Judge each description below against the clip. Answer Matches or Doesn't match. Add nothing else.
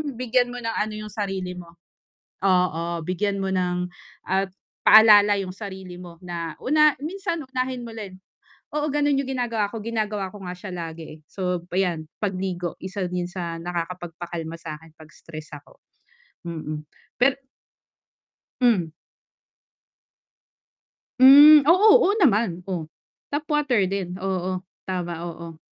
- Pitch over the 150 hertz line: Matches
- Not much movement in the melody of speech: Doesn't match